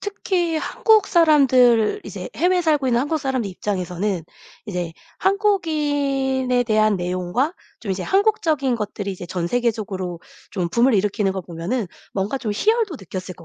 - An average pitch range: No, wide, 8.4 semitones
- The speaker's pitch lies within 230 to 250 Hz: Yes, high, 240 Hz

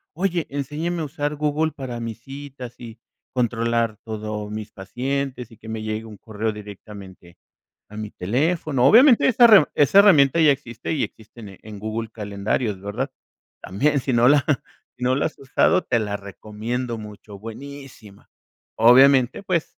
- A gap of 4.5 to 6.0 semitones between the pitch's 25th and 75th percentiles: Yes, average, 4.9 semitones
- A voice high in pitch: No, low, 120 Hz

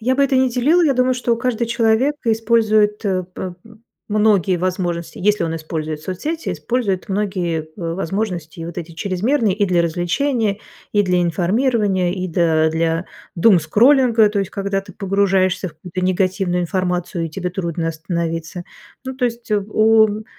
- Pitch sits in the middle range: No, high, 195 Hz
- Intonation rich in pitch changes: No, average, 4.3 semitones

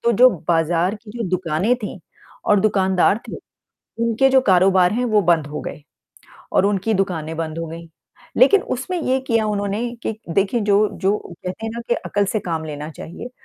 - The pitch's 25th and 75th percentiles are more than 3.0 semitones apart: Yes, average, 4.7 semitones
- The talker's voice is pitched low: No, high, 195 Hz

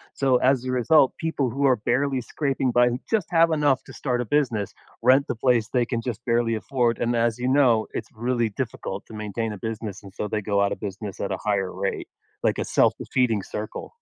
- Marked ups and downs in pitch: No, average, 3.3 semitones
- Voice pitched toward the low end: Yes, low, 120 Hz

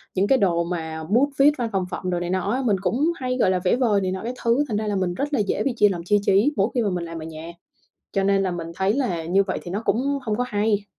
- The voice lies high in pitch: Yes, high, 200 Hz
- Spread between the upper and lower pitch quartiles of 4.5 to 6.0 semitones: Yes, average, 4.9 semitones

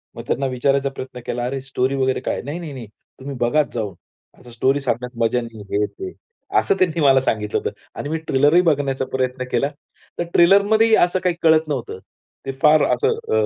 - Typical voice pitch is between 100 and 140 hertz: Yes, low, 135 Hz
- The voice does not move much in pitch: No, average, 4.0 semitones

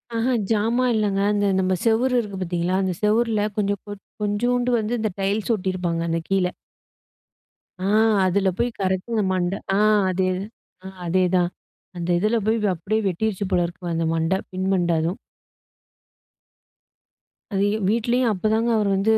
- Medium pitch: No, high, 200 Hz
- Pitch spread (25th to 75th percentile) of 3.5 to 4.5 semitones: No, average, 3.1 semitones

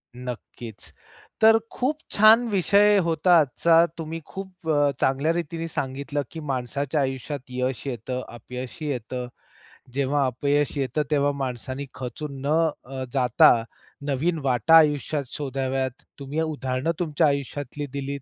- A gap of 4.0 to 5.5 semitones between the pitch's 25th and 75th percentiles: No, average, 3.6 semitones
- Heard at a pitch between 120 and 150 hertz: Yes, medium, 140 Hz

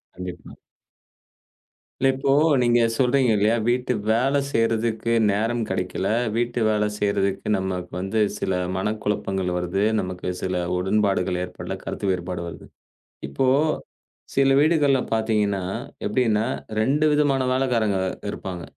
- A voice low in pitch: Yes, low, 105 Hz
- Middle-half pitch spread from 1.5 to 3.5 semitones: No, average, 4.5 semitones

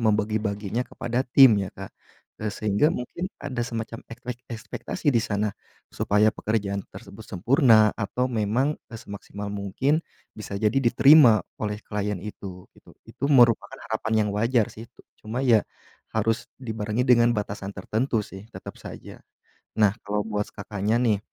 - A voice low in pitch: Yes, low, 110 Hz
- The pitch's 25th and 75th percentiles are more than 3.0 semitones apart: No, average, 2.7 semitones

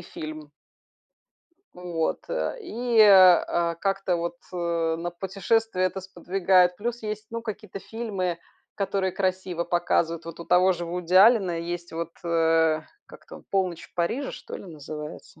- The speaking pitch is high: No, medium, 180 Hz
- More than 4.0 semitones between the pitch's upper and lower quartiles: No, narrow, 2.6 semitones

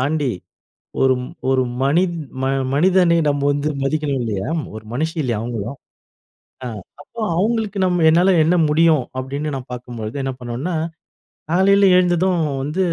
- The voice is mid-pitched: Yes, medium, 150 Hz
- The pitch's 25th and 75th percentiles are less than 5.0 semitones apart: No, wide, 5.4 semitones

